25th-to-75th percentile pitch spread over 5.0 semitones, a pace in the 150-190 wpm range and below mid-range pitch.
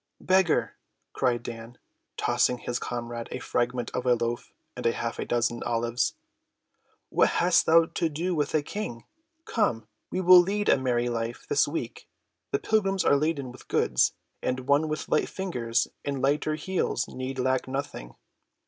Yes: wide, 5.4 semitones; average, 160 wpm; low, 130 Hz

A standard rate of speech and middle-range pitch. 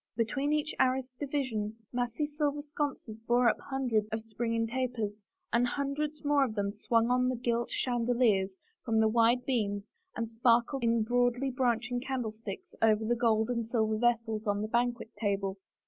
No: average, 160 wpm; high, 235 Hz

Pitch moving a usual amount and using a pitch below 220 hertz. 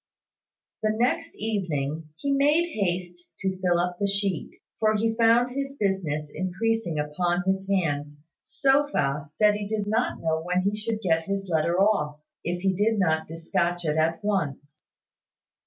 Yes: average, 4.8 semitones; high, 190 Hz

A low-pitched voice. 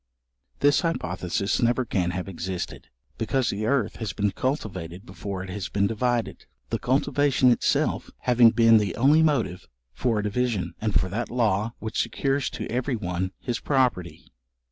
Yes: low, 110 Hz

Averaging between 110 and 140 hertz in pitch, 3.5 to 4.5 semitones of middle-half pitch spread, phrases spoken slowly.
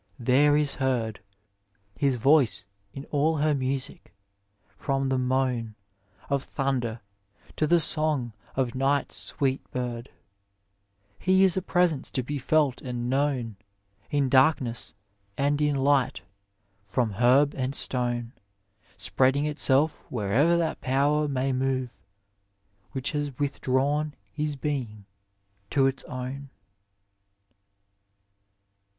No: low, 135 Hz; narrow, 2.5 semitones; slow, 120 wpm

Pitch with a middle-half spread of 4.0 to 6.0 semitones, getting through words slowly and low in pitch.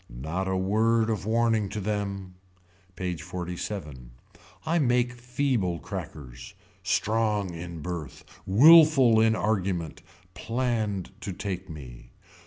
Yes: average, 4.5 semitones; slow, 110 wpm; low, 100 Hz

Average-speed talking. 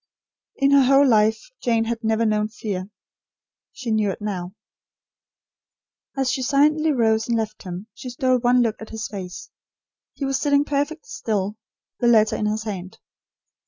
Yes: average, 160 wpm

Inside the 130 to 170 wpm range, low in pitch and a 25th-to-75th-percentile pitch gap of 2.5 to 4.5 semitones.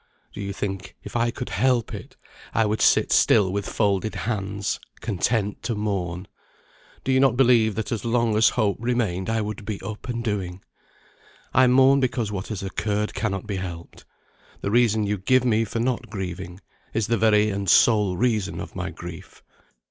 No: average, 180 wpm; low, 105 Hz; average, 3.0 semitones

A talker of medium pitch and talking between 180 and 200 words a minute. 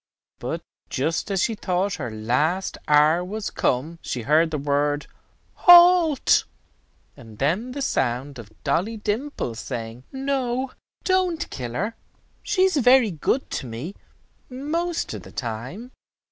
No: medium, 180 Hz; slow, 135 wpm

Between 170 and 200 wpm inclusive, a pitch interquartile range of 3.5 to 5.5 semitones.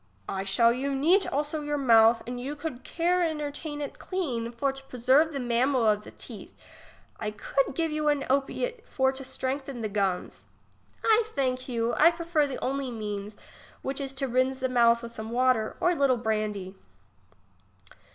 Yes: average, 180 wpm; average, 3.9 semitones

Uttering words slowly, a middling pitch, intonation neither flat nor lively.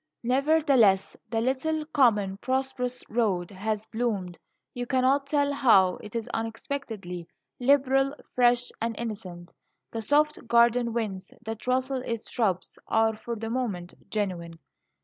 No: slow, 130 wpm; high, 235 Hz; average, 4.0 semitones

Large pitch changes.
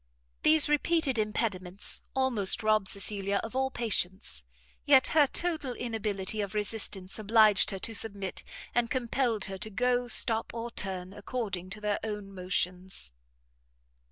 No: average, 3.9 semitones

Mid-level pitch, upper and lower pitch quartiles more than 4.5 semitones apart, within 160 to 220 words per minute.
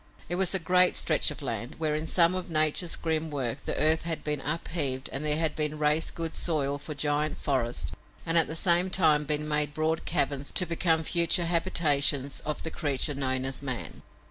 No: medium, 155 Hz; narrow, 2.6 semitones; fast, 205 wpm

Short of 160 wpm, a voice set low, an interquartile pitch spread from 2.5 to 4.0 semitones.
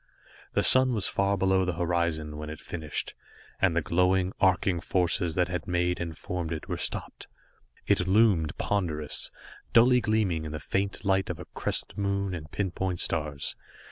No: average, 175 wpm; very low, 90 Hz; average, 3.0 semitones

